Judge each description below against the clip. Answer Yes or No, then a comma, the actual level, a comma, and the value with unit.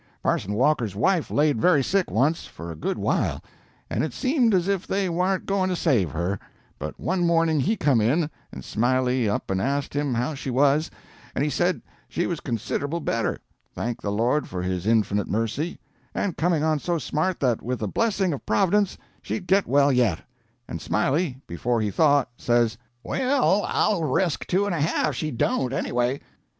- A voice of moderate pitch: Yes, medium, 145 Hz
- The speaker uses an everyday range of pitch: No, wide, 7.0 semitones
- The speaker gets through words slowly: No, average, 185 wpm